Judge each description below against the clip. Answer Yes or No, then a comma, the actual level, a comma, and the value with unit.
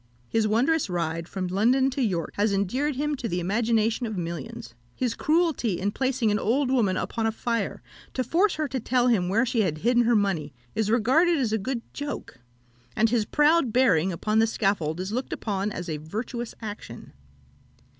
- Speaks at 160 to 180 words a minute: No, average, 190 wpm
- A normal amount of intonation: Yes, average, 4.8 semitones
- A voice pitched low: No, high, 225 Hz